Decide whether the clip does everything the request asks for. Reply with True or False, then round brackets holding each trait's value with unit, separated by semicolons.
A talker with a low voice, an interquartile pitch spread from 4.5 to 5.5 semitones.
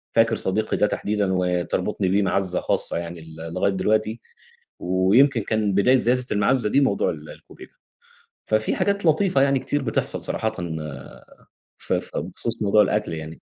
True (105 Hz; 4.8 semitones)